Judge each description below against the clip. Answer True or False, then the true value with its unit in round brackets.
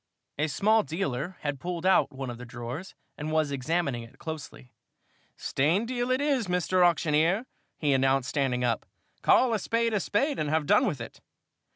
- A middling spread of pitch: False (6.4 semitones)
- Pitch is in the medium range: True (160 Hz)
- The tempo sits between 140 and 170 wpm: False (180 wpm)